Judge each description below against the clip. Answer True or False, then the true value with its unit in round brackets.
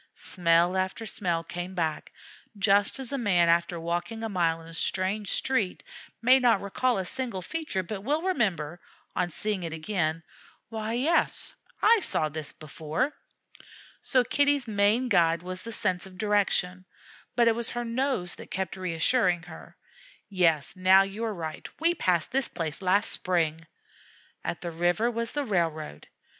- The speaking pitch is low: False (190 Hz)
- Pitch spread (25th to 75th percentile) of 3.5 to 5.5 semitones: True (5.2 semitones)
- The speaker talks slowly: False (160 wpm)